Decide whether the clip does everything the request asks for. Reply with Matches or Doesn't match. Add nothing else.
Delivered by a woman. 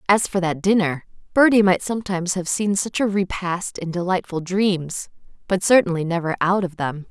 Matches